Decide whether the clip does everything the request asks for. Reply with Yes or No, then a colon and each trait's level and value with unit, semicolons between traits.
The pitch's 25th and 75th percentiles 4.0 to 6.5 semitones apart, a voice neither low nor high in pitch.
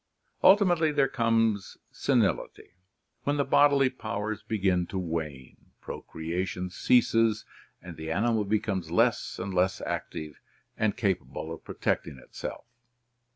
No: average, 4.6 semitones; low, 100 Hz